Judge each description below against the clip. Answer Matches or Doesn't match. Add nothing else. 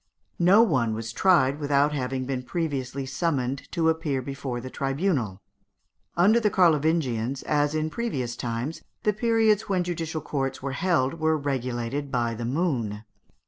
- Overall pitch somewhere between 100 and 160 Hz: Matches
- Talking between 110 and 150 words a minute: Matches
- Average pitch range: Matches